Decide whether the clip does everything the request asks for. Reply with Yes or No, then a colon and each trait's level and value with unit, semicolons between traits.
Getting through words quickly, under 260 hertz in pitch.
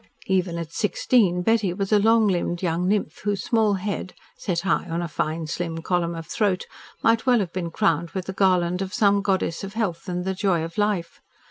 Yes: fast, 210 wpm; medium, 185 Hz